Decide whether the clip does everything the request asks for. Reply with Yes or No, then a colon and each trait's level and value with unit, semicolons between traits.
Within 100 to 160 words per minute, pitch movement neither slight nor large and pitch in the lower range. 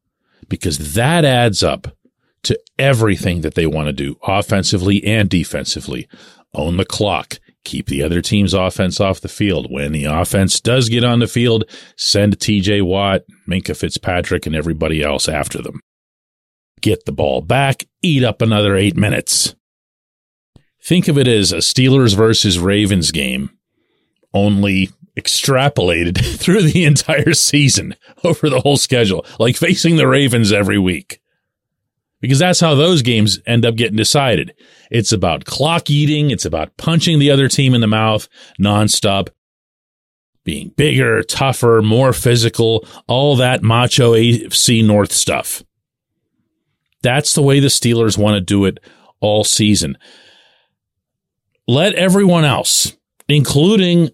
No: average, 140 wpm; wide, 5.9 semitones; low, 110 Hz